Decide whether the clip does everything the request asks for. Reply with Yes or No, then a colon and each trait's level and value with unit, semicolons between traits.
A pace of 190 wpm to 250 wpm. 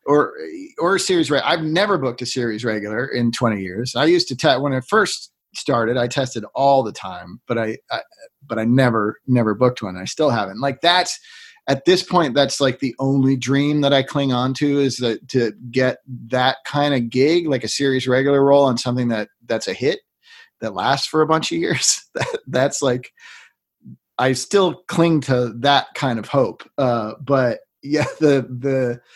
Yes: average, 200 wpm